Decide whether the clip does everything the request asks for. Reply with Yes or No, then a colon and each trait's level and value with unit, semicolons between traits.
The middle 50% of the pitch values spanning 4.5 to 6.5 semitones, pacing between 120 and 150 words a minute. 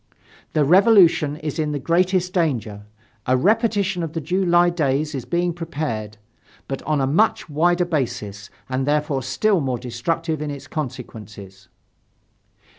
Yes: average, 5.1 semitones; average, 140 wpm